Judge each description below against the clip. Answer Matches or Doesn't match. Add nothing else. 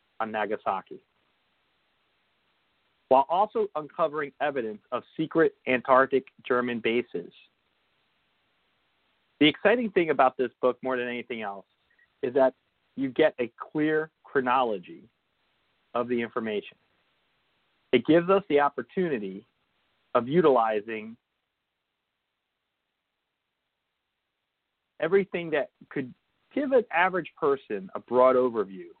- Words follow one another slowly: Matches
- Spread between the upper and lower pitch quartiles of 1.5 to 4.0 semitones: Doesn't match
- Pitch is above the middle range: Doesn't match